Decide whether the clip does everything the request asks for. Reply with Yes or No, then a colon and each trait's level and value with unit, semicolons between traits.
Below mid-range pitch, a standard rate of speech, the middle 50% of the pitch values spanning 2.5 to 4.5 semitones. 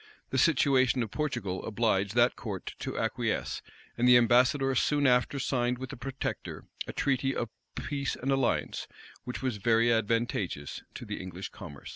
Yes: low, 125 Hz; average, 160 wpm; average, 3.1 semitones